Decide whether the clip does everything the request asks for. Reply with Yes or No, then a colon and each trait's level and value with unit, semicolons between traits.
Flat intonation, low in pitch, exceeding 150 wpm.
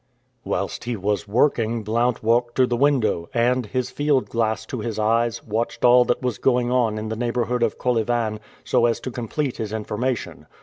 Yes: narrow, 2.1 semitones; low, 120 Hz; average, 185 wpm